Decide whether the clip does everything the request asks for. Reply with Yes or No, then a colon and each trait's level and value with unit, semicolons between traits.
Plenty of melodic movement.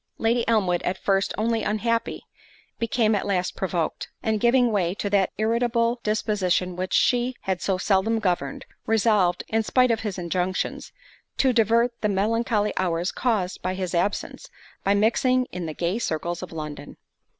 No: average, 3.9 semitones